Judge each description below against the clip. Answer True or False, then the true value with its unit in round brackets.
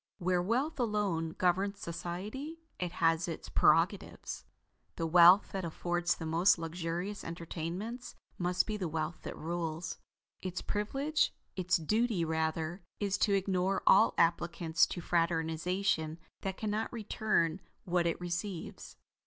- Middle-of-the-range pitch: True (180 Hz)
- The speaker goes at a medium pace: False (130 wpm)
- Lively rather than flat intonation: False (3.4 semitones)